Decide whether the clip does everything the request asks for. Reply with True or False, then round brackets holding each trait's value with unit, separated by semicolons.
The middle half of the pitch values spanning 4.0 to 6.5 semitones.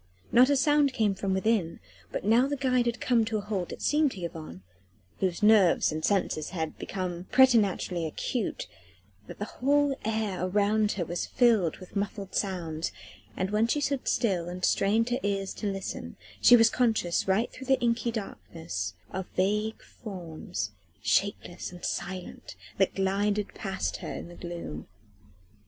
True (4.4 semitones)